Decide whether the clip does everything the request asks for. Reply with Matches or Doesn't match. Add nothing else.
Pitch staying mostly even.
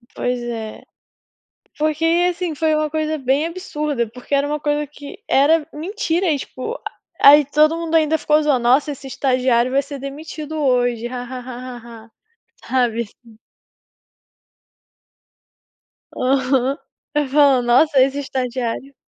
Doesn't match